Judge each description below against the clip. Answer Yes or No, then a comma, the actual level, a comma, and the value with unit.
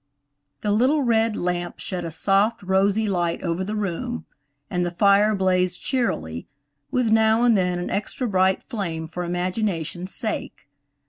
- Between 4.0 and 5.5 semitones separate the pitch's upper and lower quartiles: No, average, 3.5 semitones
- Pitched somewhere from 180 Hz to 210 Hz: Yes, high, 190 Hz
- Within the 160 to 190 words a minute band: No, average, 150 wpm